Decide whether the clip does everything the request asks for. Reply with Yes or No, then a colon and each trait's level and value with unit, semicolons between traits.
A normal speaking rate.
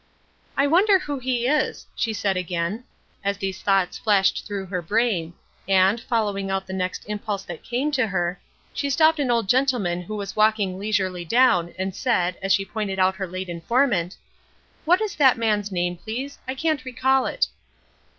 Yes: average, 180 wpm